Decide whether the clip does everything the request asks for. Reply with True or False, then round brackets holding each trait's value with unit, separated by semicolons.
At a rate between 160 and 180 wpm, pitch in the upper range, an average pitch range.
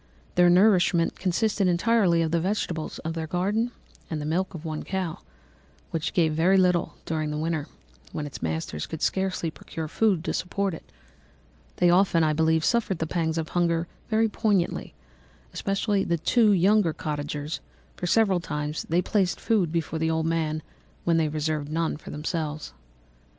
False (165 wpm; 165 Hz; 3.2 semitones)